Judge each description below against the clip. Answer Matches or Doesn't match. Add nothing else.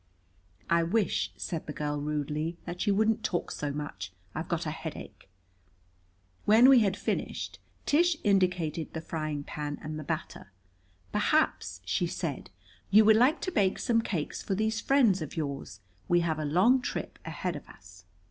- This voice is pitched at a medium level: Matches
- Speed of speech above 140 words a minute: Matches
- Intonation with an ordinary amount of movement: Doesn't match